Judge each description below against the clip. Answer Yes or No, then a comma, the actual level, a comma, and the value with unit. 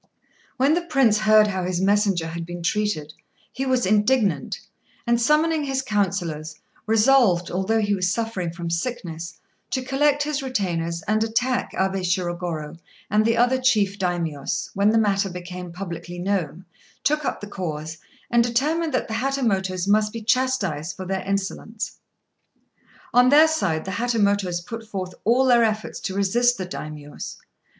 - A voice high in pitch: Yes, high, 205 Hz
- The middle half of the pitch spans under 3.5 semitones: No, wide, 5.4 semitones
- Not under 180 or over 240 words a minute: No, average, 160 wpm